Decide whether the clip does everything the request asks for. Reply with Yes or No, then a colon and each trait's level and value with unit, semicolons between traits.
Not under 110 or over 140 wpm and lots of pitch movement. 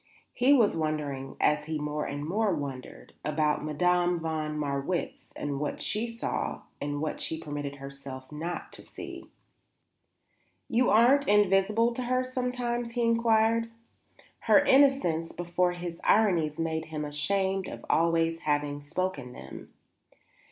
Yes: slow, 135 wpm; wide, 6.8 semitones